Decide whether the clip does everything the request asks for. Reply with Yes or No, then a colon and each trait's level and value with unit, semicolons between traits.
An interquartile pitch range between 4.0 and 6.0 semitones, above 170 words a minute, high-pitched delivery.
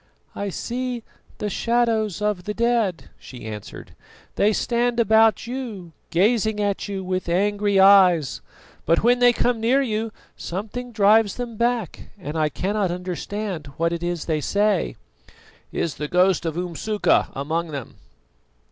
No: average, 4.5 semitones; average, 145 wpm; high, 205 Hz